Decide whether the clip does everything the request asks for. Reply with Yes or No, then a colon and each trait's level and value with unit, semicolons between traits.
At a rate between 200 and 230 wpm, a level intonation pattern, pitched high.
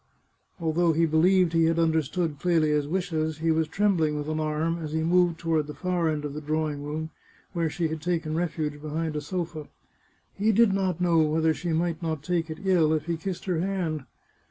No: fast, 205 wpm; narrow, 2.1 semitones; medium, 160 Hz